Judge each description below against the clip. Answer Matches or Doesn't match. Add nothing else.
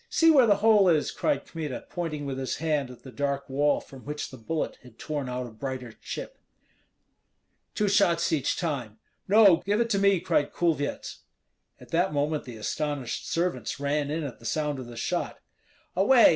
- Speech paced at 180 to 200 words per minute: Matches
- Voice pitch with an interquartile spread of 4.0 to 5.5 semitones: Matches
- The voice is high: Doesn't match